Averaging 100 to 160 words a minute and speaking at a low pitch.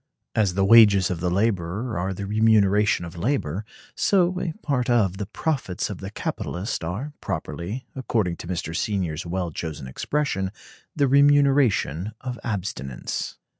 Yes: average, 145 wpm; low, 100 Hz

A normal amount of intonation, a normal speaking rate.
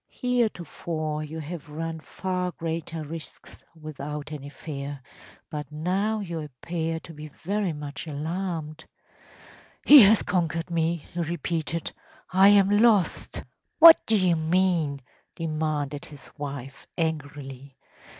No: average, 3.2 semitones; slow, 120 wpm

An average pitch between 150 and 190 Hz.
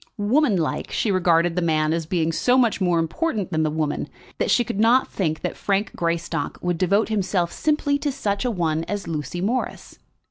Yes: medium, 185 Hz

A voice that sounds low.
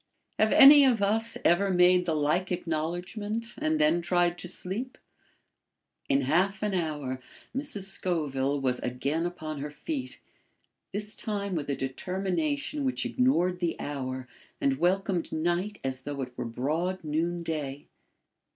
No: medium, 175 Hz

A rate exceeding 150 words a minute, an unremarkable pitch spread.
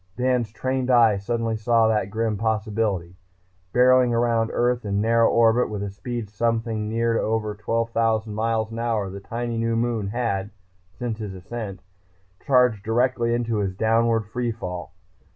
No: average, 165 wpm; narrow, 1.8 semitones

